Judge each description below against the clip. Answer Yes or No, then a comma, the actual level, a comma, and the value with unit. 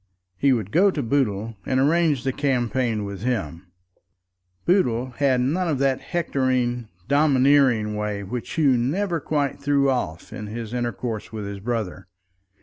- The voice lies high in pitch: No, low, 125 Hz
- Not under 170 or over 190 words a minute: No, average, 145 wpm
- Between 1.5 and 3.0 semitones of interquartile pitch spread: No, average, 4.4 semitones